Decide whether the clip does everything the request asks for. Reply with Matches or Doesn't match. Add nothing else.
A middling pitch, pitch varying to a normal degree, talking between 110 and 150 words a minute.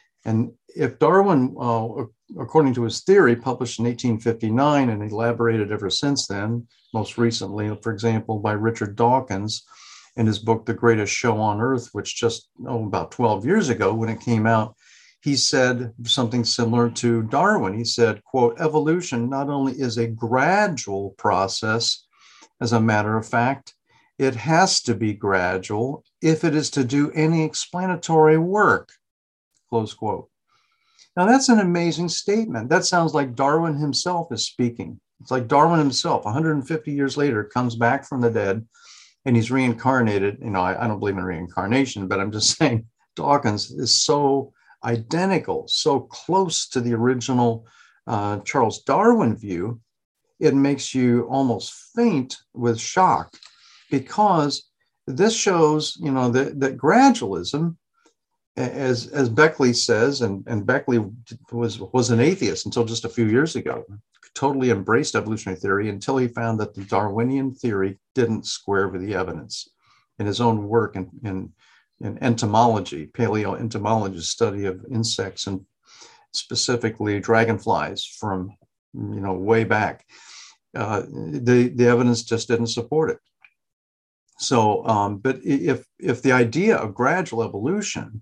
Doesn't match